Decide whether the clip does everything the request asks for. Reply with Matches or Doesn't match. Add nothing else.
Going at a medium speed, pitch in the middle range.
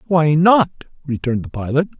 Matches